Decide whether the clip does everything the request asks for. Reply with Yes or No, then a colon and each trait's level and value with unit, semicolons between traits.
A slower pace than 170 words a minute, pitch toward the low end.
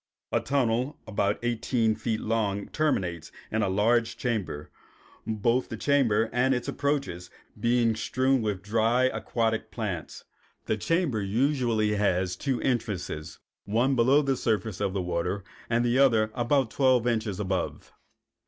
Yes: average, 140 wpm; low, 115 Hz